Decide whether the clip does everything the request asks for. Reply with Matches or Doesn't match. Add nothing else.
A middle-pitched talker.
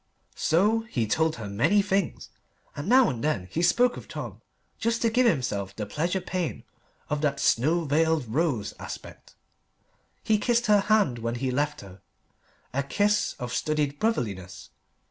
Matches